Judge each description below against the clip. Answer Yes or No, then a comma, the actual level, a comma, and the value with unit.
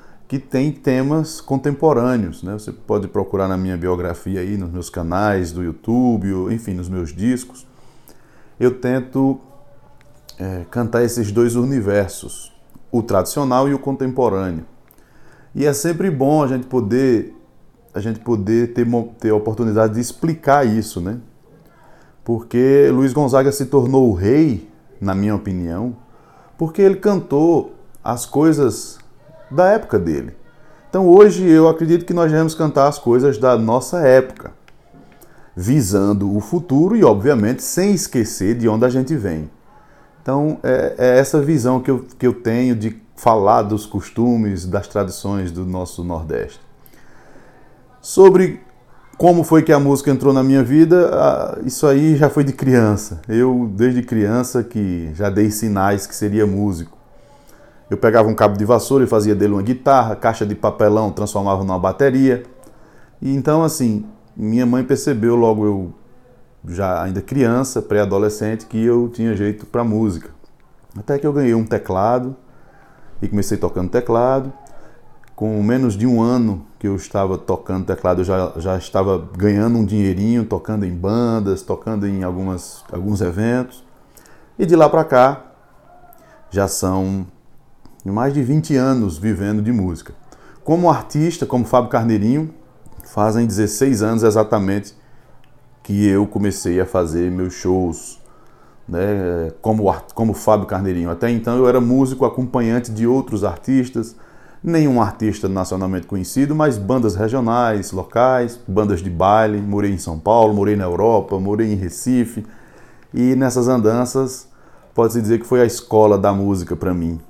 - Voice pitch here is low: Yes, low, 115 Hz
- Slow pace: No, average, 145 wpm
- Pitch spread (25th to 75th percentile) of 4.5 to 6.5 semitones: Yes, average, 4.8 semitones